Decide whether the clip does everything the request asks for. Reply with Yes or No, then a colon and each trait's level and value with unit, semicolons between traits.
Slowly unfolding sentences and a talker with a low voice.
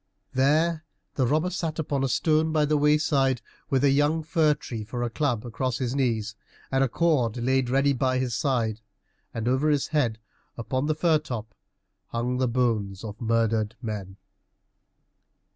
No: average, 165 wpm; low, 130 Hz